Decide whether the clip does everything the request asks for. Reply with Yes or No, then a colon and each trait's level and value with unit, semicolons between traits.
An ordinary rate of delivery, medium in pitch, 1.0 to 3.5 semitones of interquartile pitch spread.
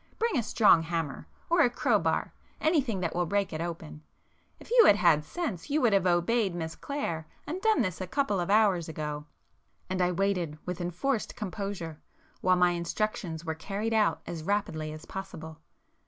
No: average, 170 wpm; medium, 180 Hz; average, 4.9 semitones